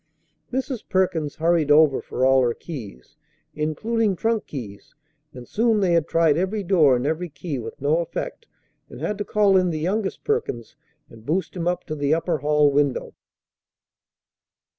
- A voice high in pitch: No, medium, 165 Hz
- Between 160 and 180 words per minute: Yes, average, 165 wpm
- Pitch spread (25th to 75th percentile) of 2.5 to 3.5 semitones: No, average, 5.0 semitones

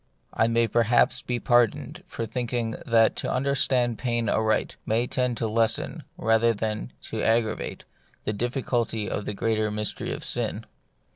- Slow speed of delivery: No, average, 150 wpm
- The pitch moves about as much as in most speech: No, narrow, 1.6 semitones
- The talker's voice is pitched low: Yes, low, 115 Hz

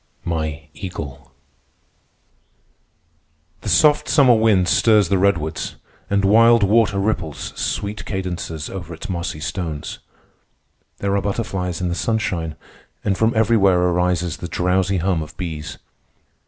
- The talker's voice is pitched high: No, very low, 95 Hz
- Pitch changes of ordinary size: Yes, average, 3.4 semitones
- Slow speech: Yes, slow, 125 wpm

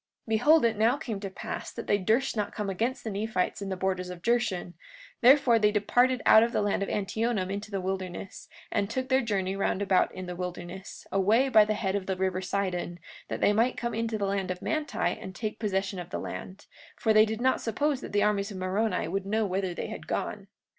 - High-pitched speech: Yes, high, 205 Hz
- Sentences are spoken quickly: Yes, fast, 230 wpm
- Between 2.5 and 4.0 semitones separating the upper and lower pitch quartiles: Yes, average, 3.2 semitones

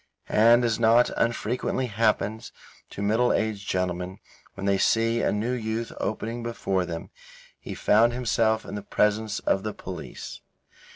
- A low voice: Yes, low, 110 Hz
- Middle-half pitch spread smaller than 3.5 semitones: Yes, narrow, 2.4 semitones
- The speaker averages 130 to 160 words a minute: Yes, average, 150 wpm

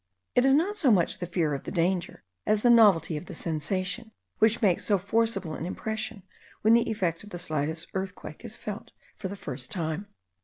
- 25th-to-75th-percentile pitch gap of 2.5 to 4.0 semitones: No, average, 4.8 semitones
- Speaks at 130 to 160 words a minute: No, average, 200 wpm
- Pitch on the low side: No, high, 190 Hz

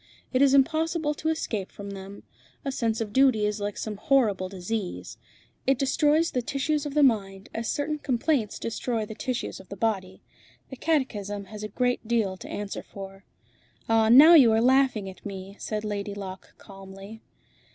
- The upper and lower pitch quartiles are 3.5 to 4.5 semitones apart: No, average, 5.1 semitones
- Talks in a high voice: Yes, high, 225 Hz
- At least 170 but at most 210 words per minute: Yes, average, 175 wpm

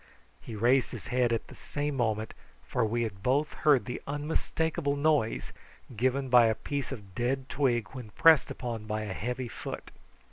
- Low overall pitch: Yes, low, 125 Hz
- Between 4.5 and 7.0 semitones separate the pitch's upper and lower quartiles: No, average, 4.1 semitones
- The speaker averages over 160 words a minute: Yes, average, 175 wpm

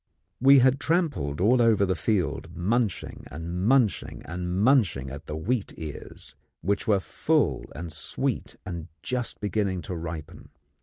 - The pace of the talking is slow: No, average, 145 wpm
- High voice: No, very low, 95 Hz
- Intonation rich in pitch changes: Yes, wide, 6.5 semitones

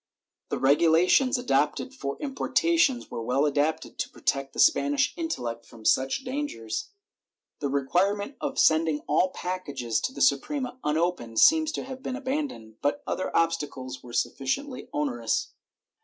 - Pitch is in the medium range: Yes, medium, 180 Hz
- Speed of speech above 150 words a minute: No, average, 140 wpm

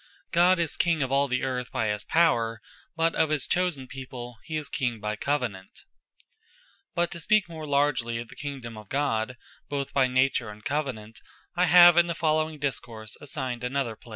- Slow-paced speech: No, average, 190 wpm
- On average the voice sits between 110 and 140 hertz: Yes, low, 135 Hz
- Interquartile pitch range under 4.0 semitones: No, average, 4.9 semitones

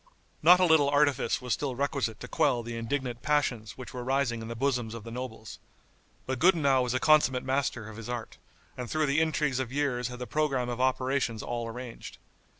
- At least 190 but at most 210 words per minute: Yes, fast, 205 wpm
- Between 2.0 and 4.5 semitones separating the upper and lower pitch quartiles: Yes, average, 3.0 semitones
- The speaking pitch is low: Yes, low, 130 Hz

